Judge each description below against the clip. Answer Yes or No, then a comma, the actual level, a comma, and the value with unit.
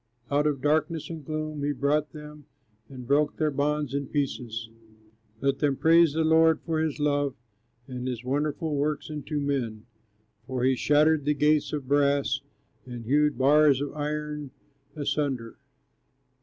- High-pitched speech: No, medium, 145 Hz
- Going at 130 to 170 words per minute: Yes, average, 150 wpm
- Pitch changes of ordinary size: No, narrow, 1.9 semitones